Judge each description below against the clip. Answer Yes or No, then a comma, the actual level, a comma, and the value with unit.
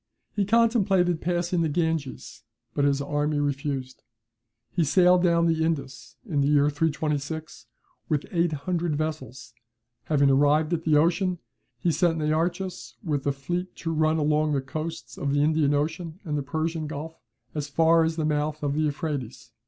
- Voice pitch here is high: No, medium, 155 Hz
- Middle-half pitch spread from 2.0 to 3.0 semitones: Yes, narrow, 2.5 semitones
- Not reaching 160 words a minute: No, average, 165 wpm